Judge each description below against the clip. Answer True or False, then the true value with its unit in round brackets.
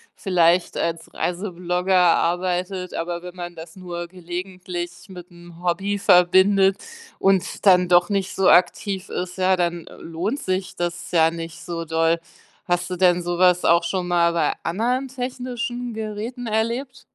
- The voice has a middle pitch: True (180 Hz)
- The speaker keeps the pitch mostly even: True (2.1 semitones)